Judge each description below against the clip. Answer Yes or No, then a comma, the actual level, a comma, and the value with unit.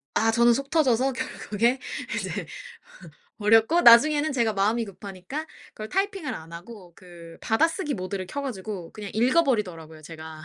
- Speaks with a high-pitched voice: Yes, high, 225 Hz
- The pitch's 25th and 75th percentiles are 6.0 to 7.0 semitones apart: Yes, wide, 6.5 semitones